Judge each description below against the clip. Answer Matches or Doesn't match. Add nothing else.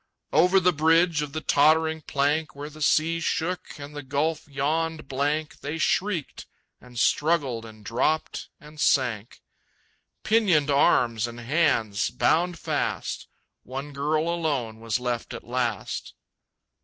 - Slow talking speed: Matches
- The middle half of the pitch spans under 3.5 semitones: Doesn't match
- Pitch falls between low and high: Matches